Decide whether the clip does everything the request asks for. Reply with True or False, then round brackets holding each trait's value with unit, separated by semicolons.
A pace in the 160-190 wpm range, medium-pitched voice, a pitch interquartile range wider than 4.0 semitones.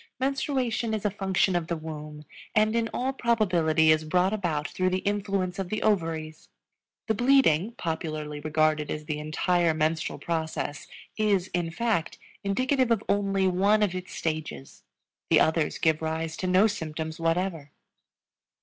False (150 wpm; 180 Hz; 4.7 semitones)